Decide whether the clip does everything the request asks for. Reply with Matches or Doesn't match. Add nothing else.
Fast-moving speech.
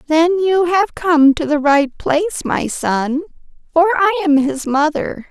Doesn't match